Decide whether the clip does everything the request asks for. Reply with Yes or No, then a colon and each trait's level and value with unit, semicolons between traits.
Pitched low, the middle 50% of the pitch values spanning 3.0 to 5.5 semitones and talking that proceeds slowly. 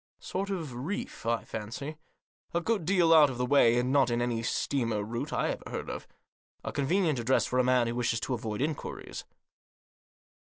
No: low, 130 Hz; average, 5.1 semitones; average, 190 wpm